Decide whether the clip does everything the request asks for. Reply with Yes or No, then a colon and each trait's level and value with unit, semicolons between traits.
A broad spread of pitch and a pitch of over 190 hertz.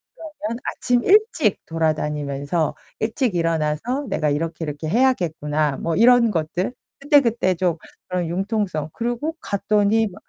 No: wide, 6.9 semitones; medium, 185 Hz